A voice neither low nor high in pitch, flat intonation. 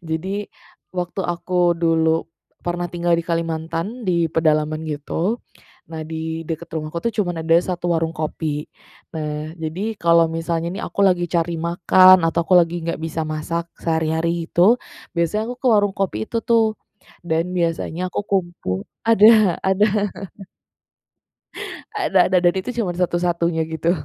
Yes: medium, 170 Hz; narrow, 1.9 semitones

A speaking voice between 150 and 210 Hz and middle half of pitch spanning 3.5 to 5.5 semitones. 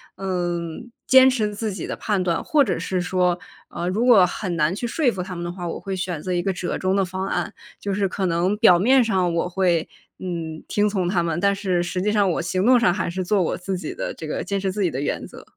No: medium, 185 Hz; average, 2.7 semitones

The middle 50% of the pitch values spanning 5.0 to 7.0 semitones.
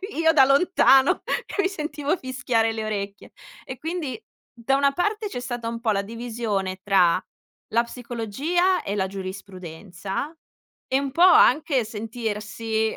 Yes: average, 5.3 semitones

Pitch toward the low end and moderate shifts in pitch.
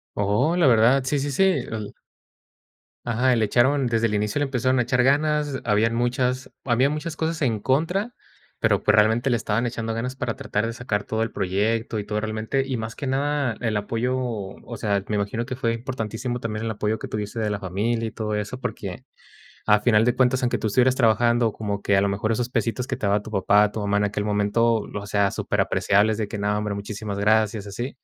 Yes: low, 115 Hz; average, 3.2 semitones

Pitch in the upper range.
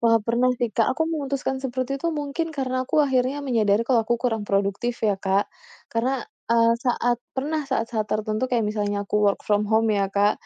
Yes: high, 235 Hz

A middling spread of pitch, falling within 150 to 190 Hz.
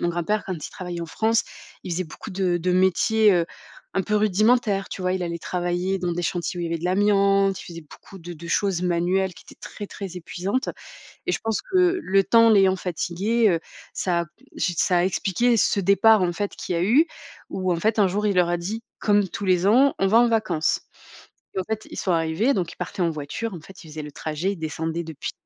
Yes: average, 3.2 semitones; medium, 185 Hz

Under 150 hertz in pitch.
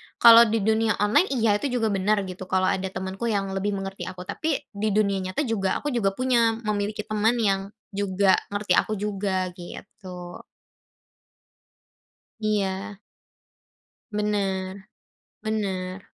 No: high, 200 Hz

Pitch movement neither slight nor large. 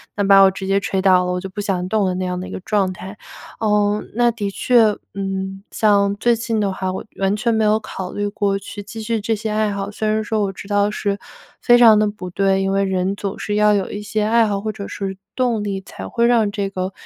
No: narrow, 1.9 semitones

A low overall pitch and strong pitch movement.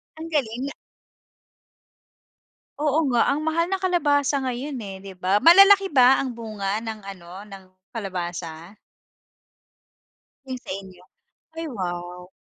No: high, 235 Hz; wide, 7.4 semitones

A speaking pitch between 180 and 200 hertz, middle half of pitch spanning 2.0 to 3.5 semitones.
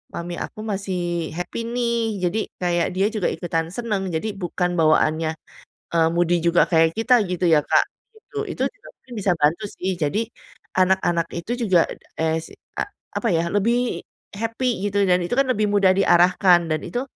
No: medium, 185 Hz; average, 4.3 semitones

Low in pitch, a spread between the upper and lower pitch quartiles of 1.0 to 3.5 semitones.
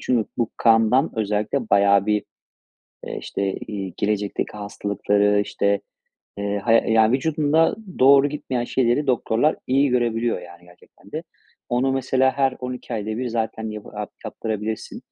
No: low, 115 Hz; average, 3.9 semitones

